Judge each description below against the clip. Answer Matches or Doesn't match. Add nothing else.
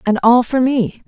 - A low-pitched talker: Doesn't match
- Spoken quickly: Matches